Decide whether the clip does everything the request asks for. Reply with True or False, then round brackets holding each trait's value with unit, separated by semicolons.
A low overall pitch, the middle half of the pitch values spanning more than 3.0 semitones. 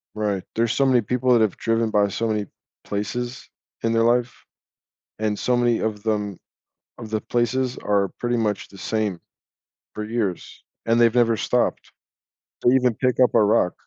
False (115 Hz; 2.5 semitones)